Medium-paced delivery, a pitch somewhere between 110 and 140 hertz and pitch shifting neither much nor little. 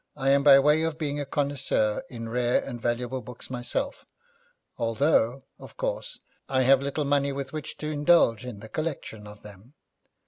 Yes: average, 175 wpm; low, 135 Hz; average, 3.5 semitones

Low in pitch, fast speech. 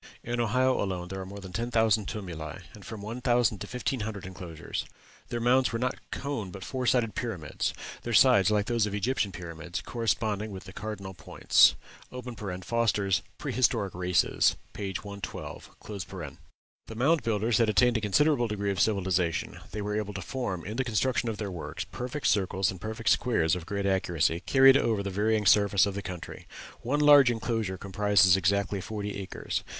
No: low, 105 Hz; average, 180 wpm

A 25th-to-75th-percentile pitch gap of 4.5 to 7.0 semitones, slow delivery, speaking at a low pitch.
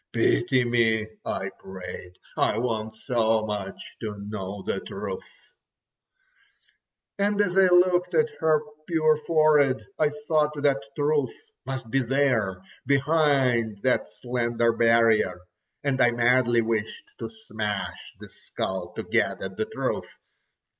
Yes: wide, 5.5 semitones; slow, 125 wpm; low, 120 Hz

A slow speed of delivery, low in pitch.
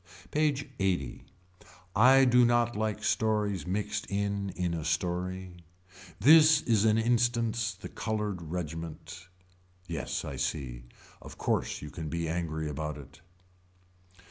Yes: slow, 125 wpm; very low, 95 Hz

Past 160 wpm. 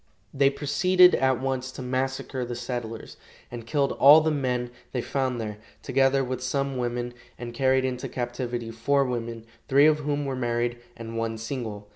Yes: average, 170 wpm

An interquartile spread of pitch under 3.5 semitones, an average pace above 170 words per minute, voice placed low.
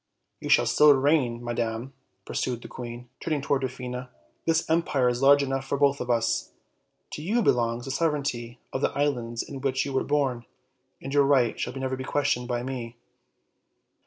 Yes: average, 2.7 semitones; average, 180 wpm; low, 130 Hz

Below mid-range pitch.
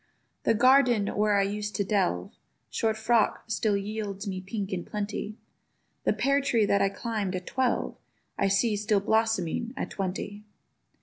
No: high, 210 Hz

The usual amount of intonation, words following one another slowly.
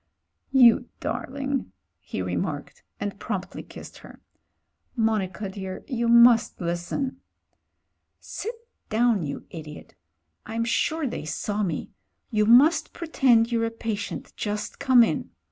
Yes: average, 4.3 semitones; slow, 125 wpm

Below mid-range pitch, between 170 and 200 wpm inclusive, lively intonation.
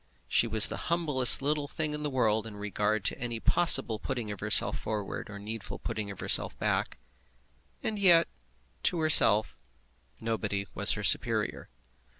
No: low, 115 Hz; average, 155 wpm; wide, 6.2 semitones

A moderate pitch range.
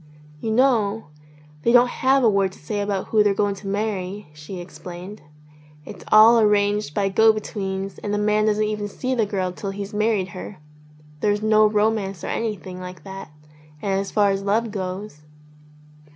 No: narrow, 1.9 semitones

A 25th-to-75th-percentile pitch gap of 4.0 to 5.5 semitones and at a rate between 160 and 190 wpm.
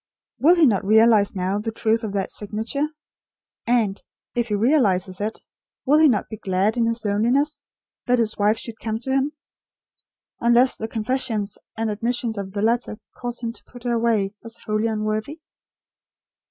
No: narrow, 2.5 semitones; average, 170 wpm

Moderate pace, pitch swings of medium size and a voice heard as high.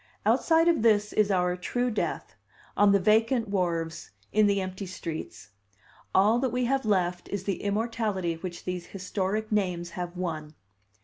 Yes: average, 160 wpm; average, 3.4 semitones; high, 200 Hz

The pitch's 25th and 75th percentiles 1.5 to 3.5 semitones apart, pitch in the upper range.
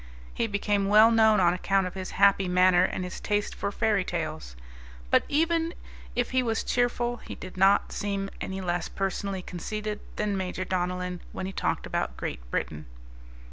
Yes: average, 2.7 semitones; high, 195 Hz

